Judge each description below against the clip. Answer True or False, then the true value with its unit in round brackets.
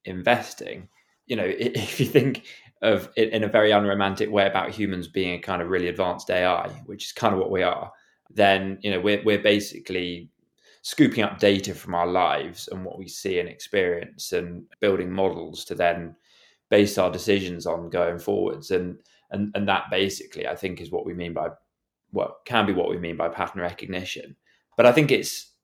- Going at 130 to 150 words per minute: False (195 wpm)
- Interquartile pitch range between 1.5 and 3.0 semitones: True (2.7 semitones)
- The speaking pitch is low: True (95 Hz)